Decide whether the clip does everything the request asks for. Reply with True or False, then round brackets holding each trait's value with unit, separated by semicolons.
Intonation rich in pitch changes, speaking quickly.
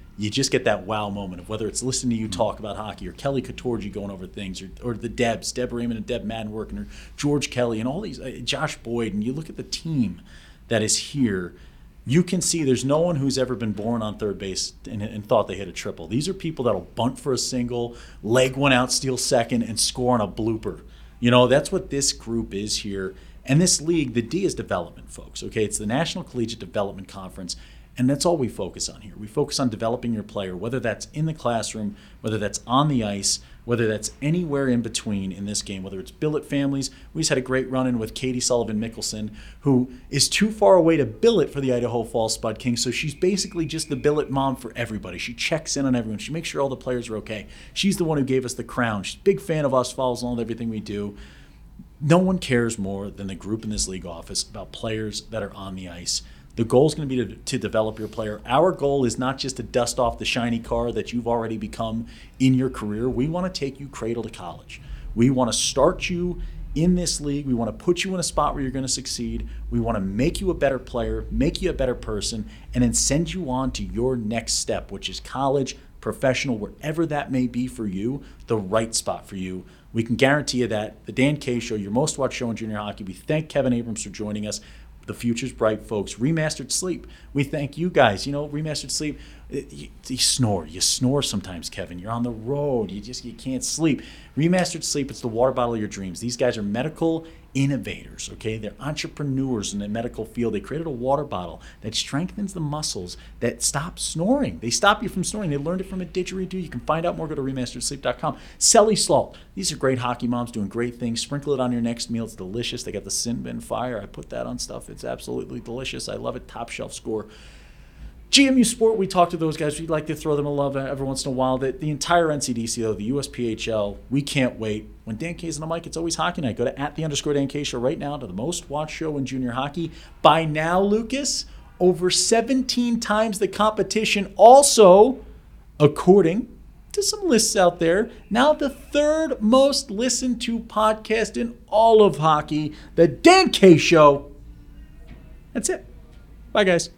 True (5.9 semitones; 225 wpm)